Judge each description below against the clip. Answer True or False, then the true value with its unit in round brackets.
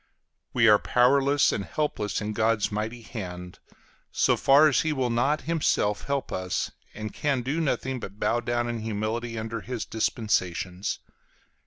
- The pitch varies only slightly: False (3.8 semitones)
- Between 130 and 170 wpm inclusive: True (155 wpm)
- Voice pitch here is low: True (115 Hz)